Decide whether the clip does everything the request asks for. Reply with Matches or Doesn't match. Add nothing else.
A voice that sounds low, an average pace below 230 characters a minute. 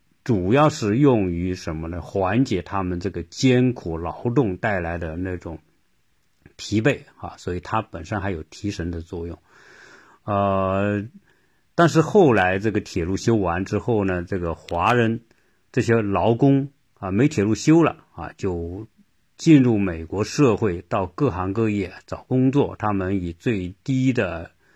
Matches